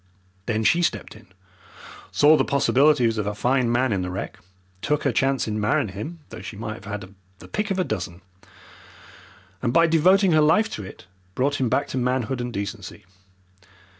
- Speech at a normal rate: Yes, average, 190 wpm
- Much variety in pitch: Yes, wide, 6.0 semitones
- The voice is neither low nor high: No, low, 125 Hz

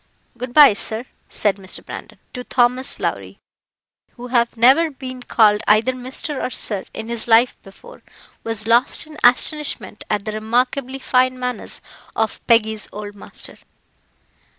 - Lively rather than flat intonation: No, average, 2.9 semitones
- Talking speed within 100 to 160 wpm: Yes, average, 145 wpm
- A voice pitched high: Yes, high, 240 Hz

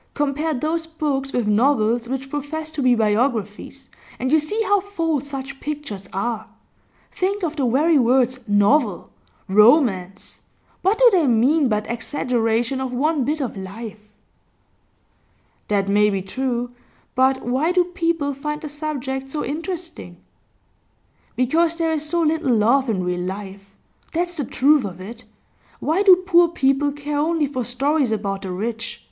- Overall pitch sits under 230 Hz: No, very high, 270 Hz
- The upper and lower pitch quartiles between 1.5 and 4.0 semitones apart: No, wide, 5.6 semitones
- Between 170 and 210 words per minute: No, average, 155 wpm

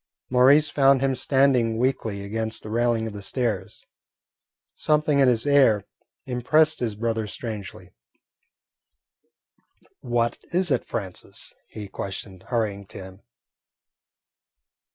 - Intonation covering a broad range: No, average, 4.1 semitones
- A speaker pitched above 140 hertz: No, low, 115 Hz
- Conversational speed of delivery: No, slow, 110 wpm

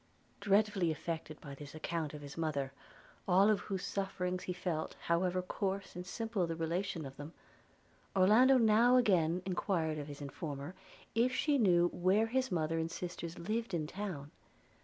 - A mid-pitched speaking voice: Yes, medium, 180 Hz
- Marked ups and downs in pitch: No, average, 4.1 semitones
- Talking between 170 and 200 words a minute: No, average, 160 wpm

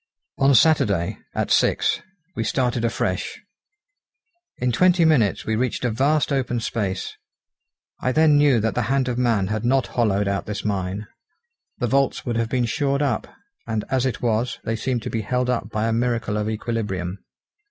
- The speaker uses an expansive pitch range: No, average, 3.4 semitones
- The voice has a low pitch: Yes, low, 120 Hz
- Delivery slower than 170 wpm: No, average, 175 wpm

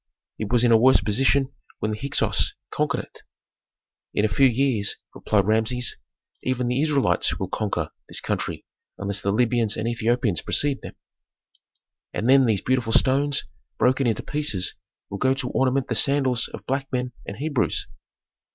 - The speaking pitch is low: Yes, low, 125 Hz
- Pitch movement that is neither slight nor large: Yes, average, 3.6 semitones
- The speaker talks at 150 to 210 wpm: Yes, average, 160 wpm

